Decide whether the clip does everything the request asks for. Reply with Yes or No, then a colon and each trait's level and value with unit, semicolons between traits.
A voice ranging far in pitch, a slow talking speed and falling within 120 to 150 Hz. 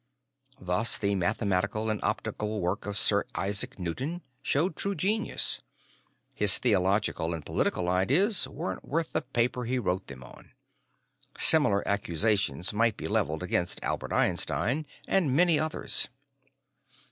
No: wide, 6.6 semitones; slow, 130 wpm; low, 105 Hz